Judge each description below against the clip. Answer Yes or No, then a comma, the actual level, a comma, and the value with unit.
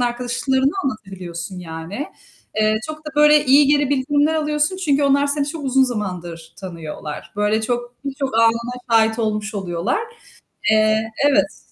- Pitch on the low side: No, high, 240 Hz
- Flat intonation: No, wide, 5.4 semitones